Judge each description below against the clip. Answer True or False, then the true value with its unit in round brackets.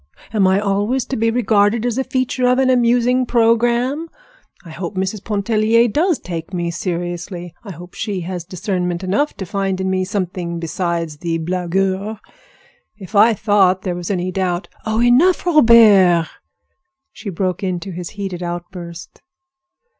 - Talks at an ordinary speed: True (155 wpm)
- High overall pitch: True (195 Hz)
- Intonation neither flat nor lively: True (4.5 semitones)